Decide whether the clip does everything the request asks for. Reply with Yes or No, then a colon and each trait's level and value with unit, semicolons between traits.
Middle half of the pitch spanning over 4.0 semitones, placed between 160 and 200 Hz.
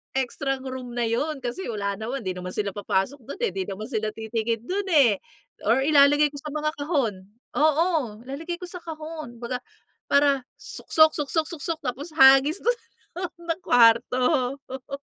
No: average, 5.0 semitones; very high, 270 Hz